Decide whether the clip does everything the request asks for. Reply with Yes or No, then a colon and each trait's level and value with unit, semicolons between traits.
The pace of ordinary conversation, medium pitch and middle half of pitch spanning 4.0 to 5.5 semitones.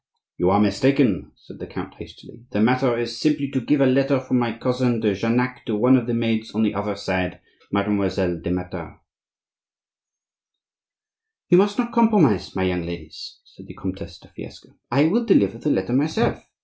No: average, 180 wpm; low, 115 Hz; average, 5.2 semitones